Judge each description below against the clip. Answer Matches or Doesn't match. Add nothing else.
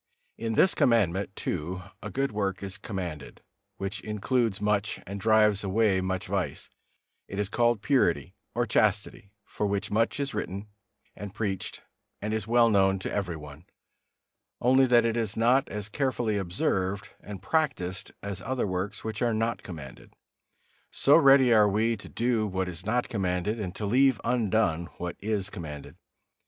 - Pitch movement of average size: Matches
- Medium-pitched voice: Doesn't match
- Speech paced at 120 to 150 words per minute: Doesn't match